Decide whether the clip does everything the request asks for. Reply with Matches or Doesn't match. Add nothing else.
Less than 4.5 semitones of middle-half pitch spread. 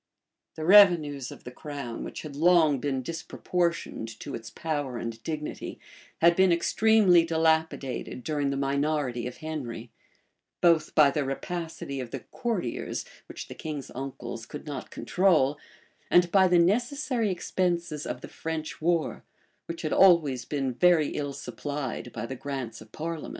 Matches